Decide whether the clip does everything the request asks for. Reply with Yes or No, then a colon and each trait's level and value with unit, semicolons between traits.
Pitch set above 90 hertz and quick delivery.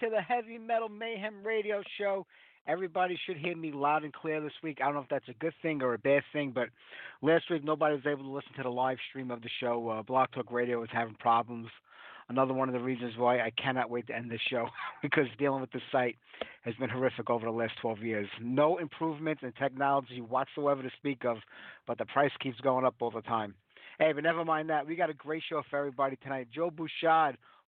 Yes: low, 135 Hz; fast, 235 wpm